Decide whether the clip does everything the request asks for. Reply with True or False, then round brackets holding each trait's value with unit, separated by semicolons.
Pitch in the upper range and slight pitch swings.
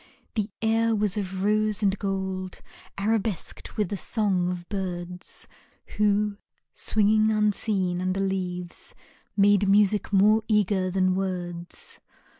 True (195 Hz; 2.3 semitones)